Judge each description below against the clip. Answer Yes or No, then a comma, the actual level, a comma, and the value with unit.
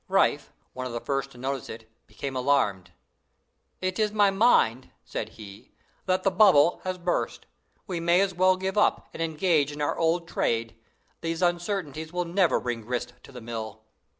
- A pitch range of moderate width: No, wide, 6.9 semitones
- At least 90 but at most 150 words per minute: No, average, 180 wpm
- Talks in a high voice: No, medium, 160 Hz